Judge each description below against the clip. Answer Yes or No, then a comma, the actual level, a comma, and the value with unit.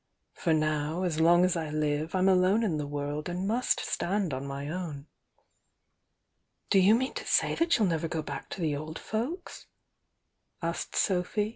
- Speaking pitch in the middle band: Yes, medium, 170 Hz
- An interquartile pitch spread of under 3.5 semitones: No, average, 4.1 semitones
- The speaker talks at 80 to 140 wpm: No, average, 180 wpm